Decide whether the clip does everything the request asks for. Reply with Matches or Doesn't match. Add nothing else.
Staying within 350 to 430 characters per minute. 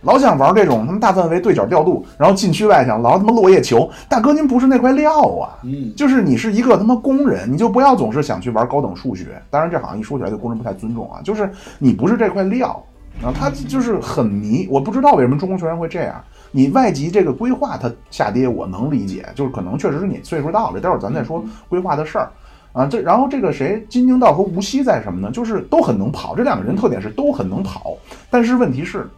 Matches